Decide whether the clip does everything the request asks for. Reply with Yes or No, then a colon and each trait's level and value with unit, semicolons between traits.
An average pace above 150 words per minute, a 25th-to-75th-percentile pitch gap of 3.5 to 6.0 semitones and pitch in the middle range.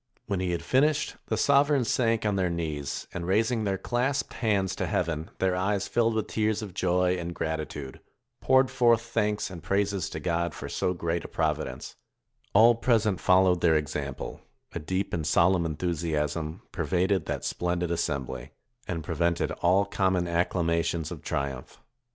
No: average, 165 wpm; average, 4.1 semitones; very low, 90 Hz